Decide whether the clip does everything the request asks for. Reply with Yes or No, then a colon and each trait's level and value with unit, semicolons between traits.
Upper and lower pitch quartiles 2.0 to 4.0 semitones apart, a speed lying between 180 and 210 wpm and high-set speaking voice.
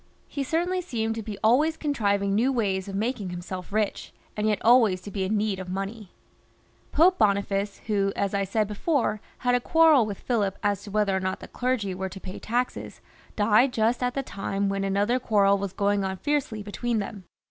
Yes: average, 3.6 semitones; average, 185 wpm; high, 210 Hz